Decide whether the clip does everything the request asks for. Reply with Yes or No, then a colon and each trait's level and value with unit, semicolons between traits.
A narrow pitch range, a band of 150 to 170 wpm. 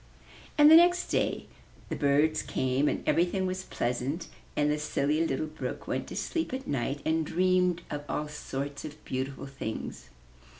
No: average, 4.5 semitones; average, 165 wpm